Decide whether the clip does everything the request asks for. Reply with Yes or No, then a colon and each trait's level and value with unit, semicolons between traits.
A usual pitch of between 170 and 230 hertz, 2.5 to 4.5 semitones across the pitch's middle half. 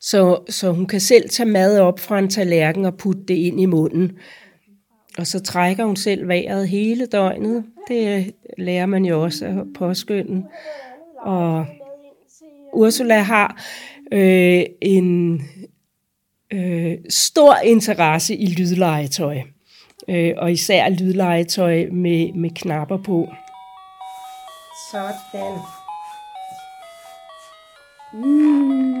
Yes: high, 190 Hz; average, 4.1 semitones